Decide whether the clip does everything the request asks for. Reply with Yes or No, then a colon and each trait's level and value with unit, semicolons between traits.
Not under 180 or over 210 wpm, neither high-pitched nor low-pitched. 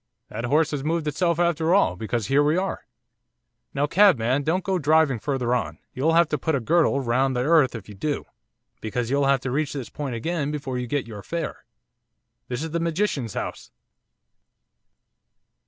Yes: average, 185 wpm; medium, 145 Hz